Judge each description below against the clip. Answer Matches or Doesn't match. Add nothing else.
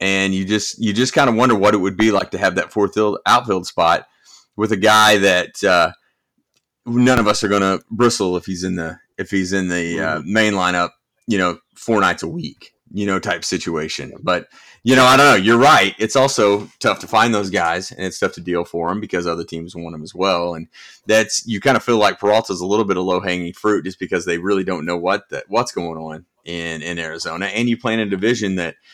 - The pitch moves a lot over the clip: Doesn't match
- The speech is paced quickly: Matches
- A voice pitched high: Doesn't match